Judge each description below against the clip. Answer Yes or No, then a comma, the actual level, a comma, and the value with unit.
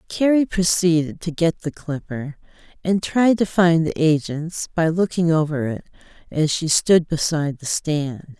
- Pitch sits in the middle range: Yes, medium, 165 Hz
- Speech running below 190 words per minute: Yes, average, 155 wpm